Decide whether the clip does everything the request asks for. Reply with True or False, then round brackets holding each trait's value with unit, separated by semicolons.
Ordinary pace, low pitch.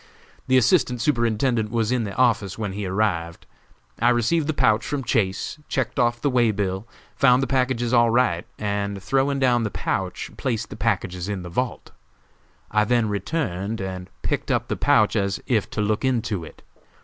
True (180 wpm; 115 Hz)